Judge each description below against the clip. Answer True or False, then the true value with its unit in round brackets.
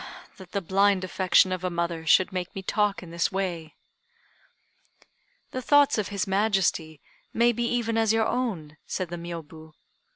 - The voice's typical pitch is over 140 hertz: True (190 Hz)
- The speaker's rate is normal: True (165 wpm)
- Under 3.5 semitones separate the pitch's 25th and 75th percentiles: False (3.8 semitones)